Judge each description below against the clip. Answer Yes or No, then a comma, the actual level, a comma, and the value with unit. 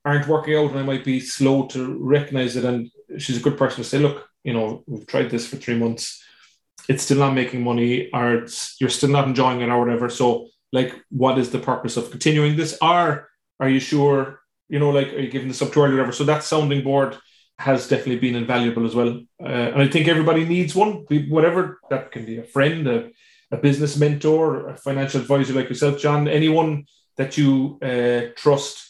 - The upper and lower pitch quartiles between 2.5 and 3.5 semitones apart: Yes, average, 2.9 semitones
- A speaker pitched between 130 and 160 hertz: Yes, low, 135 Hz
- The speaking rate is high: Yes, fast, 215 wpm